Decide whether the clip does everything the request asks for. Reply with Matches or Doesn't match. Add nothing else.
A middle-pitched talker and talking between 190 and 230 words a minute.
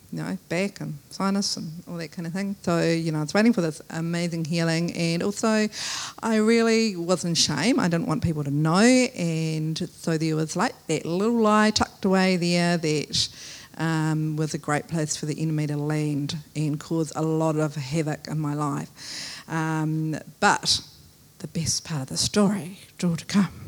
Matches